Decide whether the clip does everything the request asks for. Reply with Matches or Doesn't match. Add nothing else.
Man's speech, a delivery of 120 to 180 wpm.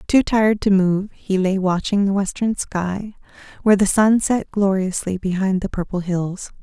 Doesn't match